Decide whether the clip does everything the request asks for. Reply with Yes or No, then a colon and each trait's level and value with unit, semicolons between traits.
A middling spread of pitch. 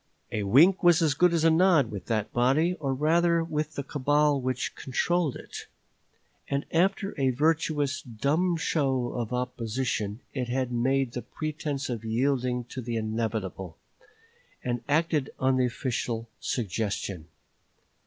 Yes: average, 4.5 semitones